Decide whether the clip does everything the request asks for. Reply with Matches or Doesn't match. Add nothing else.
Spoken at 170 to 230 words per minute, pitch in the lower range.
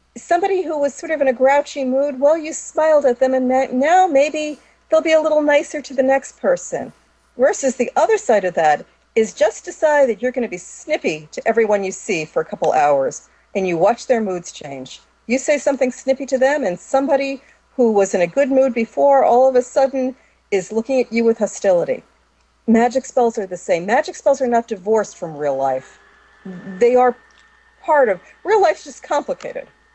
Doesn't match